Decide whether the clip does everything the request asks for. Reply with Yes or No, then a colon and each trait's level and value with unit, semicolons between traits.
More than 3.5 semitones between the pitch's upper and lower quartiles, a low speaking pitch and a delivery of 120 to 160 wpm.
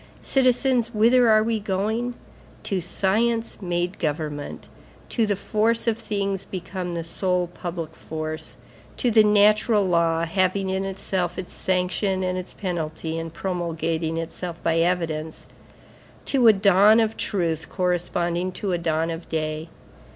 No: average, 4.0 semitones; medium, 185 Hz; average, 140 wpm